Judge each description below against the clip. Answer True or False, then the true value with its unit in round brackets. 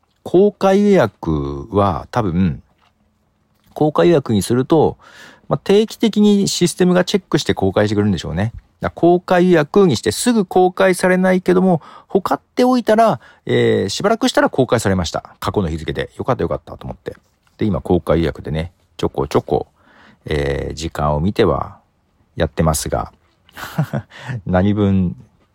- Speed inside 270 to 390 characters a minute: True (315 characters per minute)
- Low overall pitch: True (110 Hz)